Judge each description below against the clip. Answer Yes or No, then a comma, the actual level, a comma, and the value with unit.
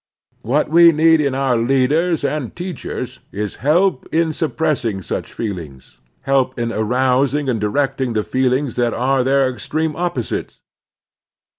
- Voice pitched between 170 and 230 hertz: No, low, 135 Hz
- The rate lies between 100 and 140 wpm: Yes, slow, 135 wpm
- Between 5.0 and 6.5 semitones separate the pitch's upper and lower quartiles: No, average, 3.9 semitones